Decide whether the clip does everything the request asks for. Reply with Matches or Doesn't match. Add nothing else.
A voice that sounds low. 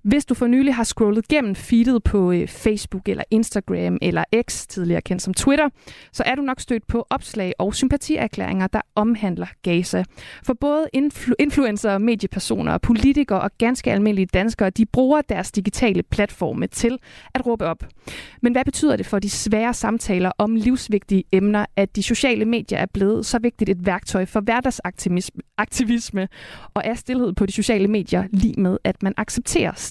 Doesn't match